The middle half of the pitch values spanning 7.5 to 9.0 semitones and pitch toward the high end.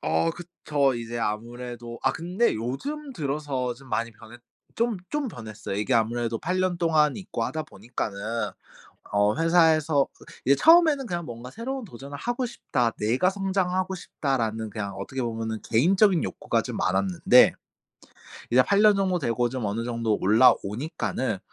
No: wide, 7.9 semitones; low, 130 Hz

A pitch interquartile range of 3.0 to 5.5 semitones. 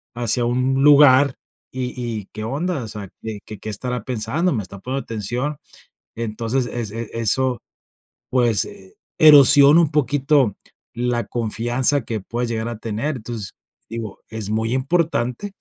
Yes: average, 3.4 semitones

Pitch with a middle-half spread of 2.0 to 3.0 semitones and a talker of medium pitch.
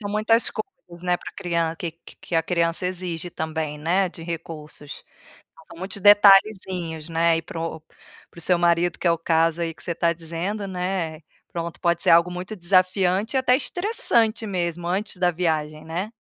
Yes: narrow, 2.5 semitones; medium, 175 Hz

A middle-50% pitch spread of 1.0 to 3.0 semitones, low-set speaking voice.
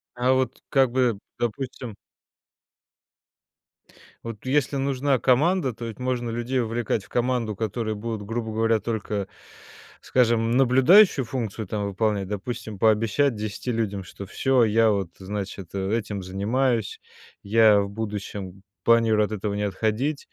No: average, 3.4 semitones; low, 115 Hz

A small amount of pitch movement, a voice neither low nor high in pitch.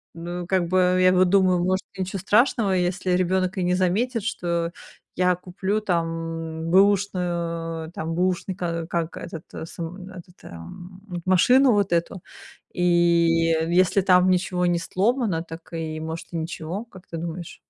Yes: narrow, 2.0 semitones; medium, 180 Hz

